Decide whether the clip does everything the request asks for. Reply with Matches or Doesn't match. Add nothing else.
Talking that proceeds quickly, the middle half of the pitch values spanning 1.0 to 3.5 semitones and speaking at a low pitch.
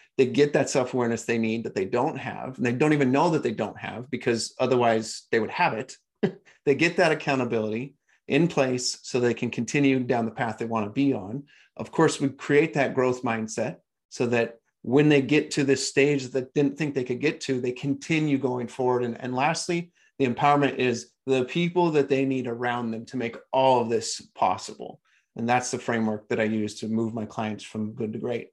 Matches